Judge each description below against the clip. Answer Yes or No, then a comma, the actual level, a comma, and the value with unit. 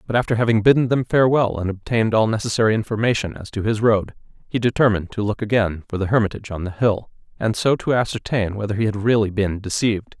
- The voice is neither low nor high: No, low, 110 Hz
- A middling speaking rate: No, fast, 210 wpm